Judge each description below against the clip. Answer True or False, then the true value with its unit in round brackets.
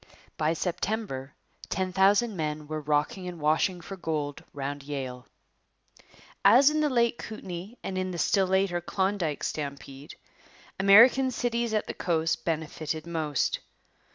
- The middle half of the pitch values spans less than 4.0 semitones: False (4.8 semitones)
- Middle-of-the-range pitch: True (175 Hz)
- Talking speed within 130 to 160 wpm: True (135 wpm)